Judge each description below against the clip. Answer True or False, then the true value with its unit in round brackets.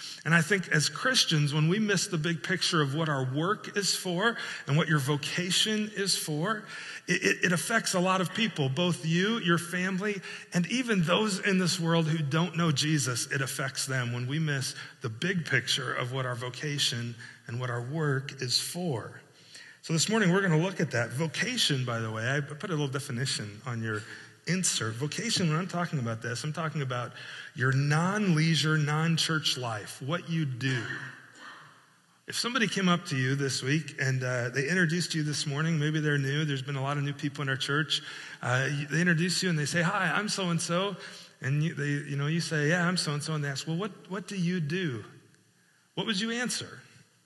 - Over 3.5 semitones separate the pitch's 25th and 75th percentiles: True (4.5 semitones)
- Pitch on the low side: False (155 Hz)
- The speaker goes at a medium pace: False (210 wpm)